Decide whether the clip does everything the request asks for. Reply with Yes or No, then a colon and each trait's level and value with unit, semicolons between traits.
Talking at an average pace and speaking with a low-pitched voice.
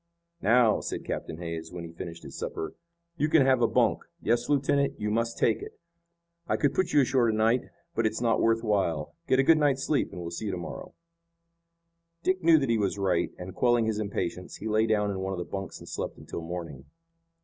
No: fast, 220 wpm; low, 110 Hz